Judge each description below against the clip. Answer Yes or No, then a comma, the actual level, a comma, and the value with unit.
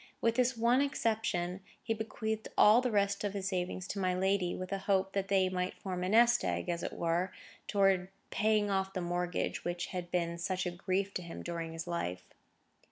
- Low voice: No, high, 190 Hz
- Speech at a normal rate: No, fast, 215 wpm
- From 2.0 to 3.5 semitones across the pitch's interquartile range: Yes, narrow, 2.6 semitones